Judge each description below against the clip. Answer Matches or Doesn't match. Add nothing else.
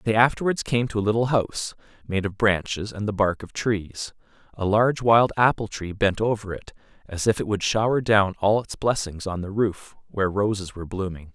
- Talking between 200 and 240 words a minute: Matches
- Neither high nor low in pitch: Doesn't match